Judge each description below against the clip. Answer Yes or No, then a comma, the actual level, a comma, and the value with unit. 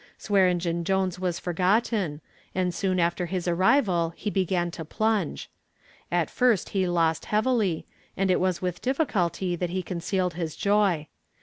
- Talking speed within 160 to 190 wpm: No, average, 145 wpm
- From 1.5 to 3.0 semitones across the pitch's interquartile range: Yes, narrow, 2.4 semitones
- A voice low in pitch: No, medium, 185 Hz